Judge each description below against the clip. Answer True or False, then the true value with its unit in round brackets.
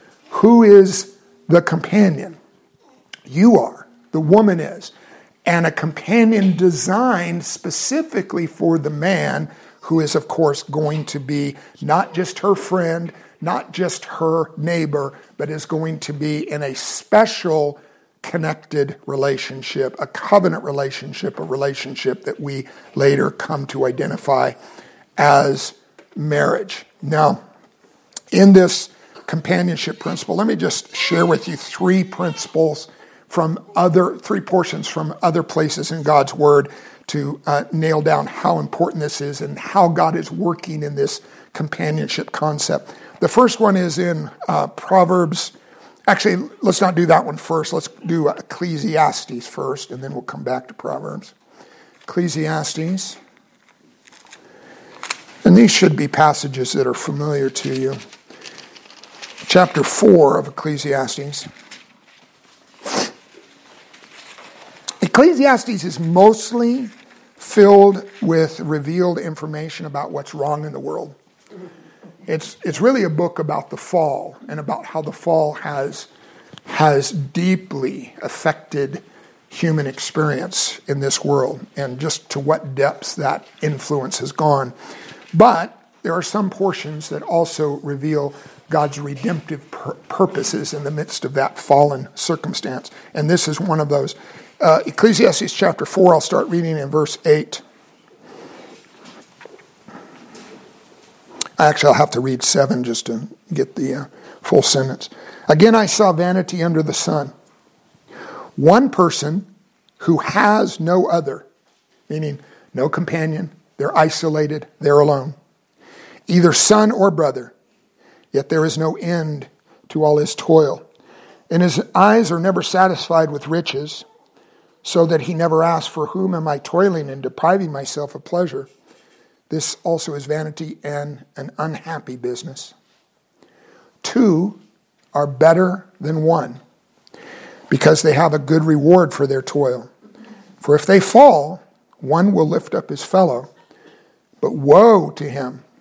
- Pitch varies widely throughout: False (3.7 semitones)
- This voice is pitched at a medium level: True (160 Hz)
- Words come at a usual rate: False (130 wpm)